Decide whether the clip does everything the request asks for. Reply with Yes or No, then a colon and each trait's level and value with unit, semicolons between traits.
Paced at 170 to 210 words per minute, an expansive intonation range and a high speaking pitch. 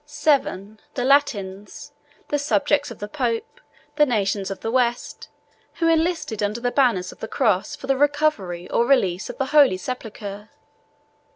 No: average, 160 wpm; wide, 6.0 semitones; high, 245 Hz